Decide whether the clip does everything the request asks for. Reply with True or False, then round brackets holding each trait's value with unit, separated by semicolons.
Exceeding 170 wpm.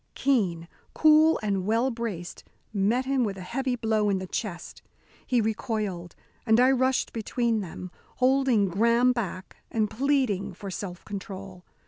False (145 wpm)